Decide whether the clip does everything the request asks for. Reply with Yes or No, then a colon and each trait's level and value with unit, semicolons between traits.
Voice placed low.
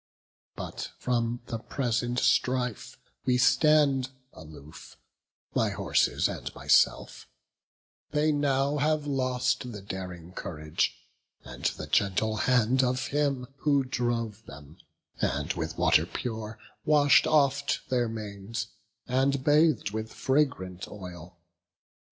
Yes: low, 125 Hz